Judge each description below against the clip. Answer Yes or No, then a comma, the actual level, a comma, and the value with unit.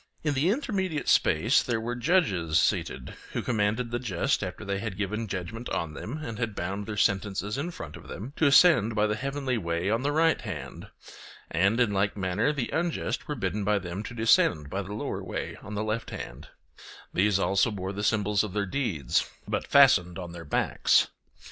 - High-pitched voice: No, low, 105 Hz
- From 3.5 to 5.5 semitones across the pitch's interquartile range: Yes, average, 4.5 semitones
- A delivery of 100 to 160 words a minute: No, average, 200 wpm